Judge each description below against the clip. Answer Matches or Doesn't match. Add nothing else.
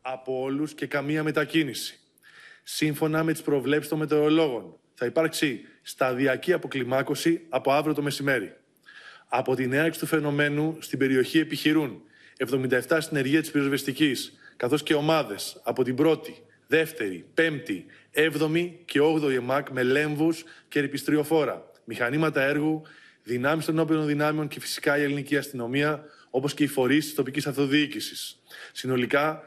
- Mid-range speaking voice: Matches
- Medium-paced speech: Matches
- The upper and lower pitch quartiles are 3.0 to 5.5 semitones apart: Doesn't match